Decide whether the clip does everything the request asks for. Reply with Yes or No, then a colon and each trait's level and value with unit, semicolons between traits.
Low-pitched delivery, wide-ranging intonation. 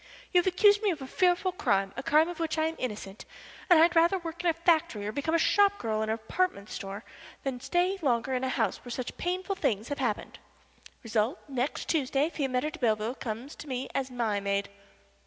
No: very high, 275 Hz; wide, 7.1 semitones